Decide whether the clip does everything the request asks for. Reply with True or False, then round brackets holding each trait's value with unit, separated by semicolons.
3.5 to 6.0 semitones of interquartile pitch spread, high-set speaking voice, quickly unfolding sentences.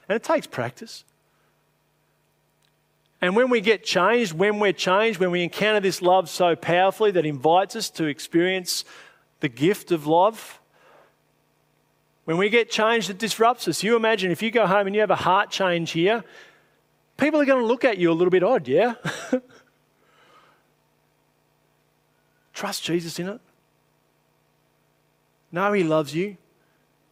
False (4.5 semitones; 195 Hz; 150 wpm)